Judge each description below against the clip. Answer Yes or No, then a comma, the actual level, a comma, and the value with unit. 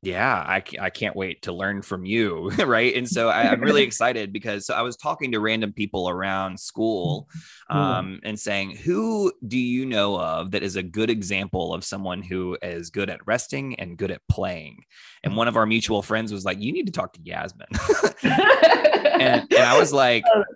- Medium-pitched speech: No, low, 105 Hz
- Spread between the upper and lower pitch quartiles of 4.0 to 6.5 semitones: No, average, 3.5 semitones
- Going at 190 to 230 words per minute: Yes, average, 200 wpm